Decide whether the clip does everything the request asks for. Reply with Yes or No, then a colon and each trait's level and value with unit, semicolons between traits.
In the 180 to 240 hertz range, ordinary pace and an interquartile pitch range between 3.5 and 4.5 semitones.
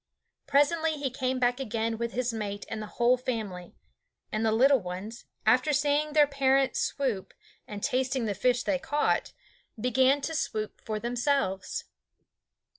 No: very high, 250 Hz; average, 150 wpm; average, 4.0 semitones